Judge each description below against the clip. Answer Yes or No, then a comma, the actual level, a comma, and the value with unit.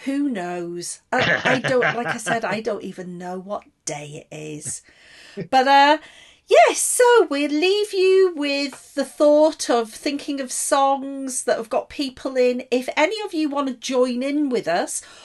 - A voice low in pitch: No, very high, 275 Hz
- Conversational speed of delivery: Yes, average, 180 wpm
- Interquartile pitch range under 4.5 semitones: No, average, 5.1 semitones